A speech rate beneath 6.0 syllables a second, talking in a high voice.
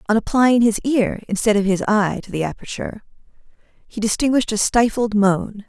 Yes: 5.3 syllables/s; high, 215 Hz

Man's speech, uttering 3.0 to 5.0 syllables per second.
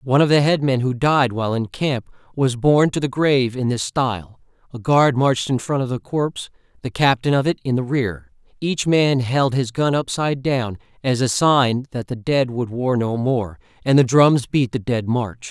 Yes: male; 4.8 syllables/s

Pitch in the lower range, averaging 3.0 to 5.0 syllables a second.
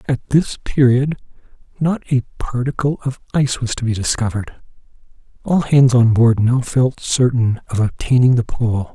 Yes: low, 125 Hz; 4.7 syllables/s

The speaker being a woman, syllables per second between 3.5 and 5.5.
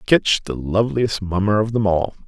No: male; 5.0 syllables/s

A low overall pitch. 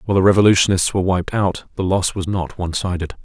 Yes: very low, 95 Hz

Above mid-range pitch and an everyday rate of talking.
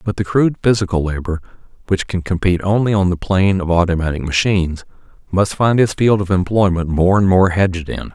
No: very low, 95 Hz; average, 190 wpm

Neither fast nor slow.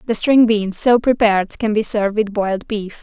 No: fast, 220 wpm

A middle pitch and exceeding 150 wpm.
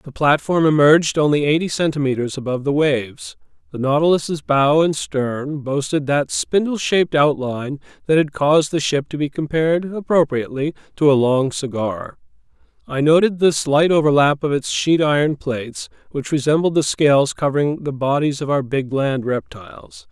Yes: medium, 145 Hz; average, 160 wpm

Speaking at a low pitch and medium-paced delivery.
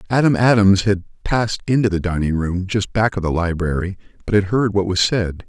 No: low, 100 Hz; fast, 210 wpm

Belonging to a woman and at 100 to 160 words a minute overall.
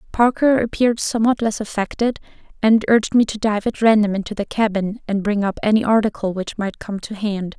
No: female; average, 200 wpm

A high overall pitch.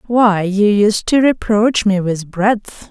Yes: high, 205 Hz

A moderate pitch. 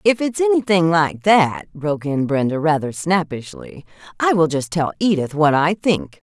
Yes: medium, 170 Hz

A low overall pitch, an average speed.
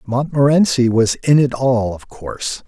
Yes: low, 125 Hz; average, 155 wpm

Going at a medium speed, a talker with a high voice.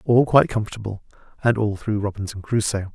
No: average, 165 wpm; low, 105 Hz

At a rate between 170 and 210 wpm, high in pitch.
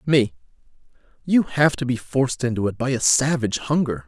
No: average, 175 wpm; low, 125 Hz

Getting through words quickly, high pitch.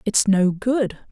No: average, 160 wpm; high, 210 Hz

